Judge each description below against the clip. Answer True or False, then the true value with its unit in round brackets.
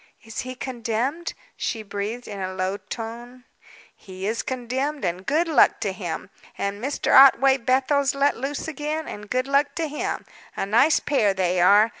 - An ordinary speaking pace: True (170 wpm)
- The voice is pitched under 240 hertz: False (250 Hz)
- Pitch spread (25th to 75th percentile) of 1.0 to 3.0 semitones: False (5.3 semitones)